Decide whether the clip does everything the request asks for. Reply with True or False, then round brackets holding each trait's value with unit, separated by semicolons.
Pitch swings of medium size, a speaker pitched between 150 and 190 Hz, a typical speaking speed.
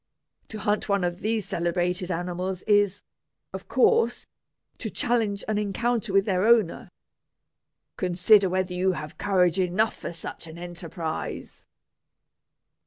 False (3.0 semitones; 185 Hz; 125 wpm)